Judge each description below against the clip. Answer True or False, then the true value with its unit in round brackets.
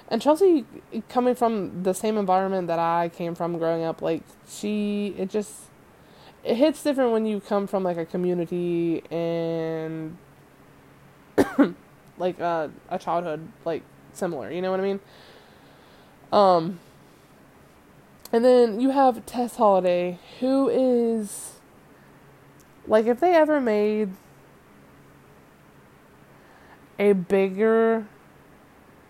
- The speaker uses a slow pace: True (115 wpm)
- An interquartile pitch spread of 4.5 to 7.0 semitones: True (4.8 semitones)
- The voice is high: True (200 Hz)